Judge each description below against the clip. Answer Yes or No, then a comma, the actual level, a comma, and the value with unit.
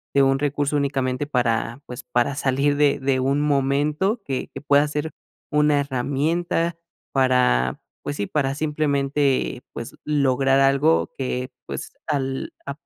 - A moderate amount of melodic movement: No, narrow, 1.8 semitones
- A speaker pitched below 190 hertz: Yes, medium, 140 Hz